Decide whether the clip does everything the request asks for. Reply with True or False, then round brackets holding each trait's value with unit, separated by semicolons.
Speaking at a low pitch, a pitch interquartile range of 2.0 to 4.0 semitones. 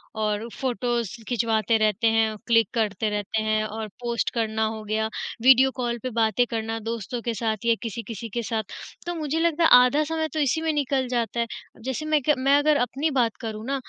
False (235 Hz; 3.3 semitones)